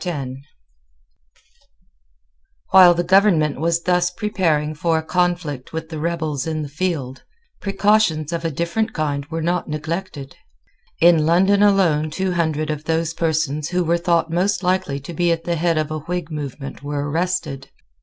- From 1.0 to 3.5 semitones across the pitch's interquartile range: Yes, average, 2.7 semitones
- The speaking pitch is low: No, medium, 165 Hz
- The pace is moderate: Yes, average, 155 wpm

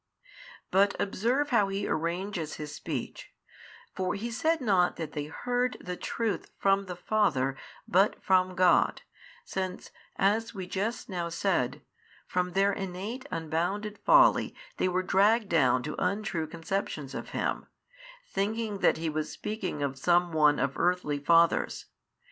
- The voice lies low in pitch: No, medium, 185 Hz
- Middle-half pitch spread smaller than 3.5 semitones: No, average, 4.0 semitones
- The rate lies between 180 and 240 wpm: No, average, 145 wpm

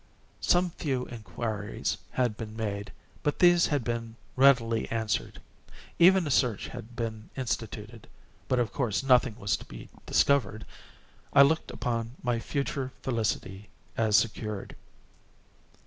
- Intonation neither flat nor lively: Yes, average, 3.5 semitones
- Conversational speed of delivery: No, slow, 125 wpm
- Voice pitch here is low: Yes, low, 115 Hz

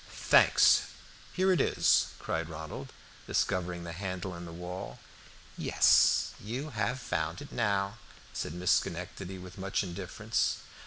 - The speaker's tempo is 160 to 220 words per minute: No, slow, 135 wpm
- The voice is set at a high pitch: No, very low, 90 Hz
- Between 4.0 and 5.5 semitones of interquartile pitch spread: No, average, 2.9 semitones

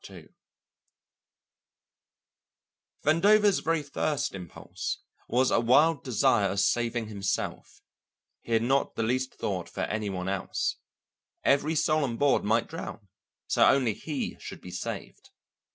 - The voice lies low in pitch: Yes, low, 125 Hz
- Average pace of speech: No, slow, 125 wpm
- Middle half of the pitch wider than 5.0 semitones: Yes, wide, 5.4 semitones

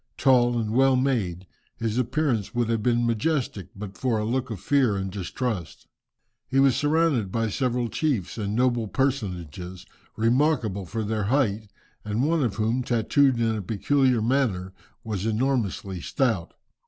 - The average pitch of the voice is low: Yes, low, 115 Hz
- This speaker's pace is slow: No, average, 155 wpm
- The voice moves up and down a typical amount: Yes, average, 4.2 semitones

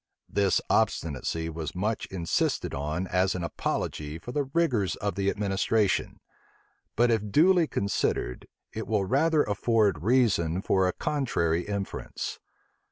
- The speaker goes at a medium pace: No, slow, 130 wpm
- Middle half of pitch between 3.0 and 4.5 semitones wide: No, average, 5.0 semitones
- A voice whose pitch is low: Yes, low, 100 Hz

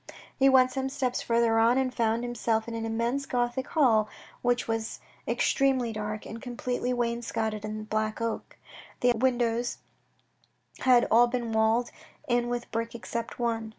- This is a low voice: No, high, 235 Hz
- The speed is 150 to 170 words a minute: Yes, average, 155 wpm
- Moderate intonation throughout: No, narrow, 1.6 semitones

